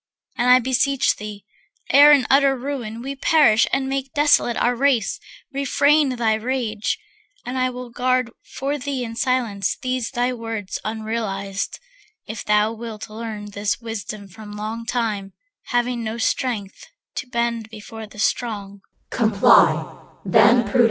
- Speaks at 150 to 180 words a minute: No, slow, 135 wpm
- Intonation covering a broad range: No, average, 3.1 semitones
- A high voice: Yes, high, 235 Hz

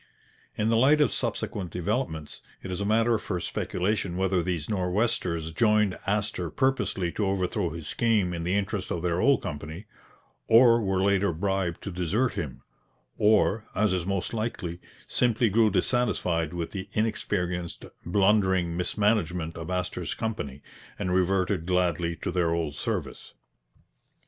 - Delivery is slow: No, average, 145 wpm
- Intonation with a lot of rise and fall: No, average, 3.6 semitones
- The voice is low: Yes, very low, 95 Hz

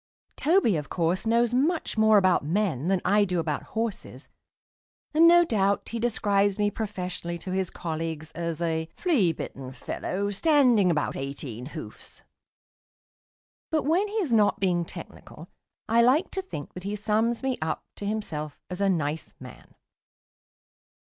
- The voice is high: Yes, high, 200 Hz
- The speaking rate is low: No, average, 155 wpm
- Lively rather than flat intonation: Yes, wide, 5.8 semitones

